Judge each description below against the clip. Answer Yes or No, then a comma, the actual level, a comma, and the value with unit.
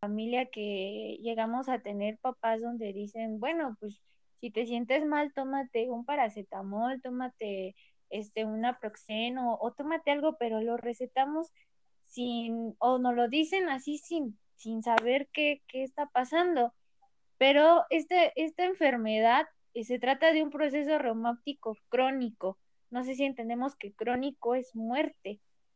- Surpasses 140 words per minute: No, average, 135 wpm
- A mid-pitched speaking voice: No, high, 245 Hz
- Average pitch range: Yes, average, 4.1 semitones